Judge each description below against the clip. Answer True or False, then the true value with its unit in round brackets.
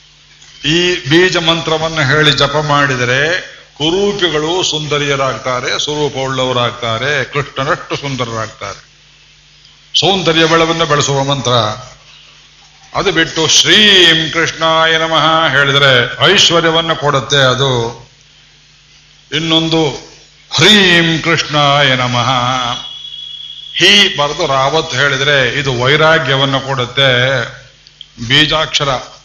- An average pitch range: True (3.2 semitones)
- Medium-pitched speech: True (145 Hz)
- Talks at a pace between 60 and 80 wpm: True (75 wpm)